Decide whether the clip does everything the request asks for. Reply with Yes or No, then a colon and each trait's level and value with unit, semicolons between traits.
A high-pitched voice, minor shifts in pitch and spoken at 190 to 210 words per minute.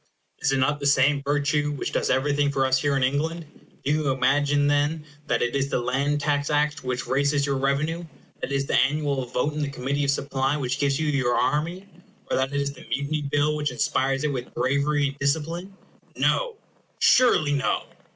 No: medium, 140 Hz; narrow, 1.5 semitones; fast, 205 wpm